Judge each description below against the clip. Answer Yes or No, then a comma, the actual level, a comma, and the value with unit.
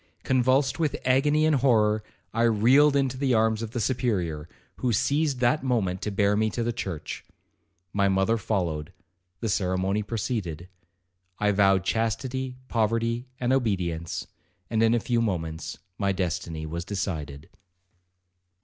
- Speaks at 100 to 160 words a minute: Yes, average, 140 wpm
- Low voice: Yes, low, 110 Hz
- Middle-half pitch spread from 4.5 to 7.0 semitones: Yes, average, 5.1 semitones